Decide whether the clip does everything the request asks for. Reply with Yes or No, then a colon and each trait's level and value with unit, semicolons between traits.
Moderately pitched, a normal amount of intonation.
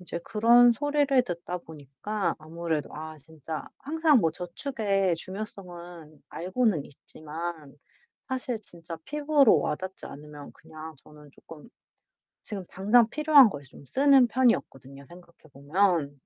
No: medium, 175 Hz; wide, 7.2 semitones